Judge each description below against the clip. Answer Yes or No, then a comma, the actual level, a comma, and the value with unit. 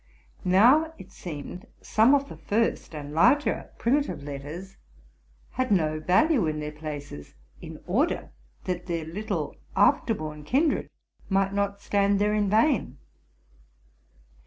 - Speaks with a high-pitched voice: Yes, high, 195 Hz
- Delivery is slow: Yes, slow, 130 wpm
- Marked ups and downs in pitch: Yes, wide, 6.6 semitones